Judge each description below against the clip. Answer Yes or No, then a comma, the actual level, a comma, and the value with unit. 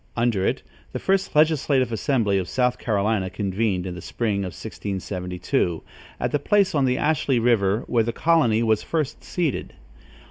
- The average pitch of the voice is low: Yes, low, 115 Hz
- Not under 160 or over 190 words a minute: Yes, average, 165 wpm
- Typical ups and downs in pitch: No, wide, 5.9 semitones